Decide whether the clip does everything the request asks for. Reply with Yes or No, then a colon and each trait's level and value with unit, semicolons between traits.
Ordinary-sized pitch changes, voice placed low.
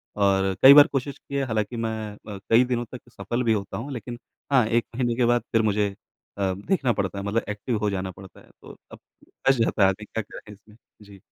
Yes: average, 3.3 semitones; low, 110 Hz